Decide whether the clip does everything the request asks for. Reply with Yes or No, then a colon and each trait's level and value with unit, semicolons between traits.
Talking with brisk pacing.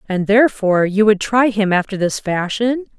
No: average, 180 wpm